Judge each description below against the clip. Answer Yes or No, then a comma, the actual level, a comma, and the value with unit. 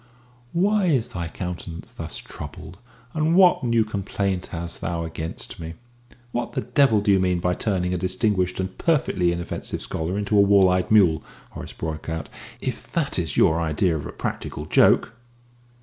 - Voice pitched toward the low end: Yes, very low, 95 Hz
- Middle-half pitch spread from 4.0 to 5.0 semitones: Yes, average, 4.3 semitones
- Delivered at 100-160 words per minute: No, average, 170 wpm